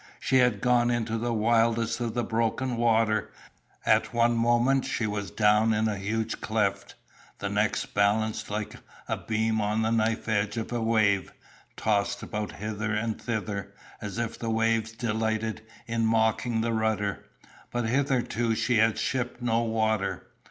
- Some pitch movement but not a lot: No, narrow, 1.4 semitones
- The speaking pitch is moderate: No, low, 110 Hz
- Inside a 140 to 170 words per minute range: Yes, average, 160 wpm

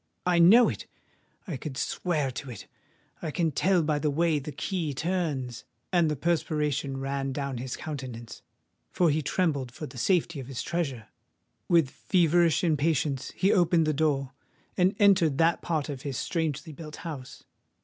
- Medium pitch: Yes, medium, 155 Hz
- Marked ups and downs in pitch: No, average, 3.9 semitones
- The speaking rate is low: No, average, 160 wpm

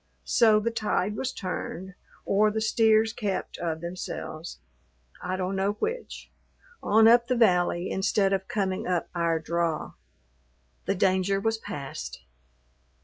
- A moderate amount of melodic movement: Yes, average, 3.5 semitones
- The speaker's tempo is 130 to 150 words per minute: Yes, slow, 135 wpm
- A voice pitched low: No, high, 195 Hz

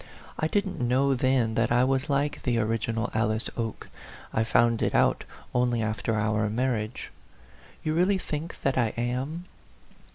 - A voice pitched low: Yes, low, 120 Hz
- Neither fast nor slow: Yes, average, 155 wpm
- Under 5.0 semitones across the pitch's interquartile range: Yes, average, 3.6 semitones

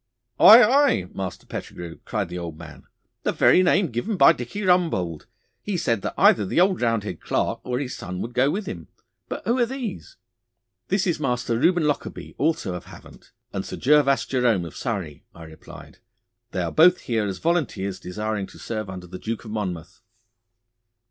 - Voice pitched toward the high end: No, low, 115 Hz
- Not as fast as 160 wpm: No, average, 180 wpm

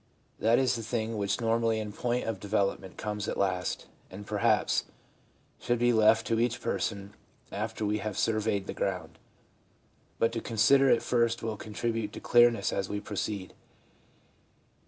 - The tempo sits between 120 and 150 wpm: No, average, 160 wpm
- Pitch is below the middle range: Yes, low, 110 Hz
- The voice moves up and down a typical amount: No, narrow, 2.2 semitones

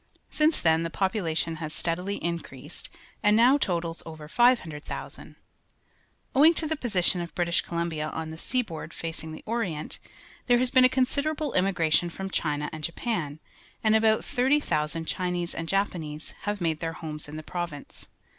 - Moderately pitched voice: Yes, medium, 175 Hz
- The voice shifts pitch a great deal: Yes, wide, 5.8 semitones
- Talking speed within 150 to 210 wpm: Yes, average, 165 wpm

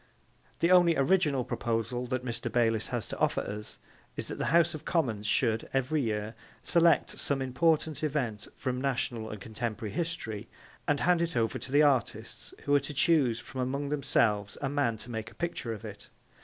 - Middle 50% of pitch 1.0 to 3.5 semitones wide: No, average, 4.8 semitones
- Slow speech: No, average, 185 wpm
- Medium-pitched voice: No, low, 130 Hz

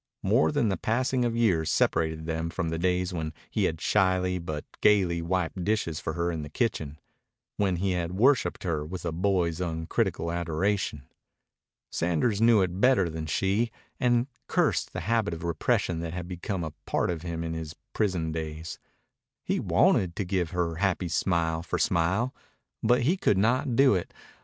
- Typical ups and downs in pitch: Yes, average, 3.6 semitones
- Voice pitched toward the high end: No, very low, 90 Hz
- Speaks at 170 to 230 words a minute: Yes, average, 175 wpm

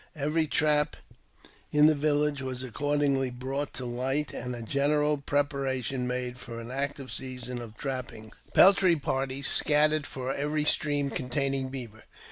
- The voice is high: No, low, 135 Hz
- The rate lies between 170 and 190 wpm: No, average, 145 wpm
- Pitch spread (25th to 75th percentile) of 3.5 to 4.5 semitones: No, narrow, 2.6 semitones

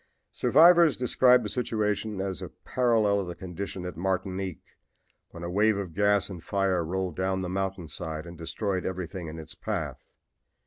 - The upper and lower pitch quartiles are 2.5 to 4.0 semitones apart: Yes, average, 2.8 semitones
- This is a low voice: Yes, very low, 95 Hz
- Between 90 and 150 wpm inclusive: No, average, 170 wpm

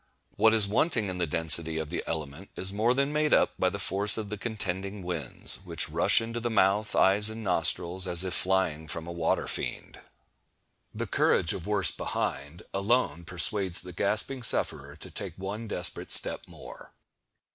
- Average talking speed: Yes, average, 180 wpm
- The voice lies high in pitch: No, very low, 95 Hz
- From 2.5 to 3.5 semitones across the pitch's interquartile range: No, average, 3.9 semitones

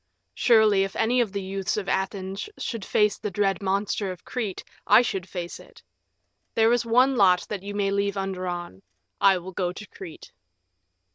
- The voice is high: Yes, high, 195 Hz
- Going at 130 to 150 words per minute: No, average, 180 wpm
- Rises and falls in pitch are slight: Yes, narrow, 2.1 semitones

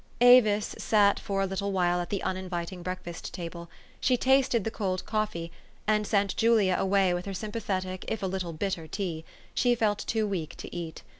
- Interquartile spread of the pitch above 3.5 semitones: No, average, 3.2 semitones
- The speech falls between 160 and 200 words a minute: Yes, average, 190 wpm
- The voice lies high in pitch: Yes, high, 195 Hz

